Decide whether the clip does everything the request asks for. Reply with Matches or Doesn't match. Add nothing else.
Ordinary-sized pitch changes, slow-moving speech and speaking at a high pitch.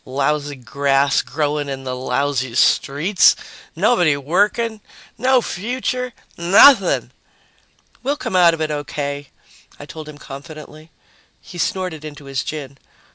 Doesn't match